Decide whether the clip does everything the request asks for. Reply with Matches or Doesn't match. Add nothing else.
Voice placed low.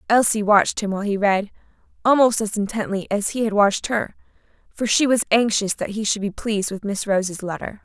Doesn't match